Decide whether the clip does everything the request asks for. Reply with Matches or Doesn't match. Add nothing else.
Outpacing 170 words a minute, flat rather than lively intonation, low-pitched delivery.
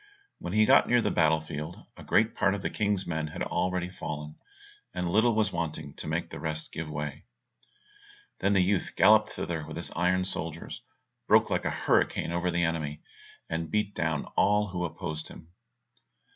Doesn't match